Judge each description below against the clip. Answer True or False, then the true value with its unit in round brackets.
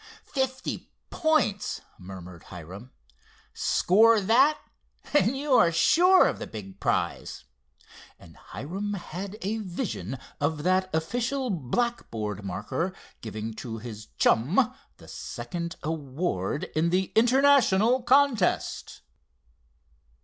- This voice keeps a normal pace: False (105 wpm)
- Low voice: False (185 Hz)